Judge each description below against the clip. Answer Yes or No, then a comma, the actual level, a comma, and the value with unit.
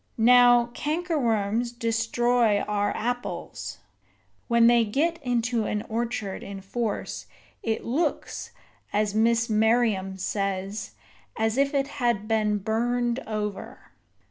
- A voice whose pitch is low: No, high, 230 Hz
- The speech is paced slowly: Yes, slow, 110 wpm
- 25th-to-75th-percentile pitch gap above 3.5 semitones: No, narrow, 2.5 semitones